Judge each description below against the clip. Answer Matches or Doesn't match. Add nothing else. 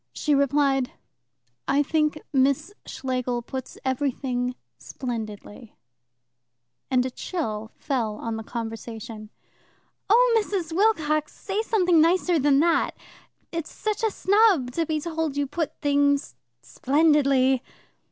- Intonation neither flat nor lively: Matches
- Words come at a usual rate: Doesn't match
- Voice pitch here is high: Matches